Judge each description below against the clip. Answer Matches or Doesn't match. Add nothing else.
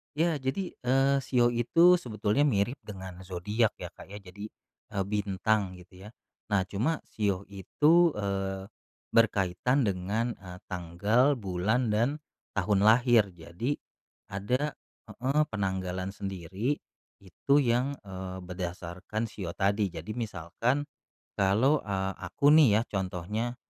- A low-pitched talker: Matches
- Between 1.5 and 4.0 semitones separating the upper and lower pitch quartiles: Doesn't match